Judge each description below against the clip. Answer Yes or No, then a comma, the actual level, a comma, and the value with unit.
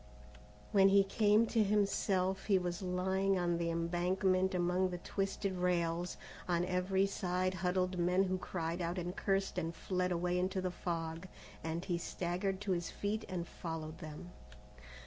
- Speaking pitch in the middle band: Yes, medium, 180 Hz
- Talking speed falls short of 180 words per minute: Yes, average, 160 wpm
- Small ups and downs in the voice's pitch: Yes, narrow, 1.7 semitones